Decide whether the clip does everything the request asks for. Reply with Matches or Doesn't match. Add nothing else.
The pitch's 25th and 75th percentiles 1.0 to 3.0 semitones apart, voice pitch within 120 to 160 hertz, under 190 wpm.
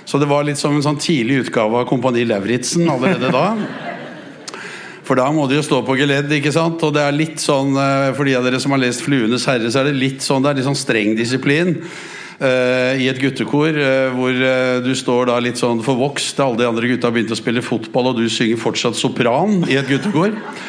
Doesn't match